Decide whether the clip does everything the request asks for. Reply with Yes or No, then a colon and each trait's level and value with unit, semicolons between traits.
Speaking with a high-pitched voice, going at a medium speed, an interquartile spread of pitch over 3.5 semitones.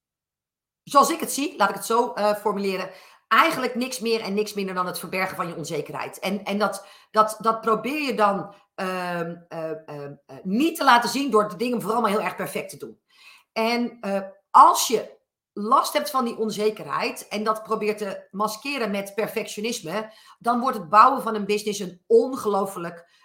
No: high, 215 Hz; average, 185 wpm; average, 3.0 semitones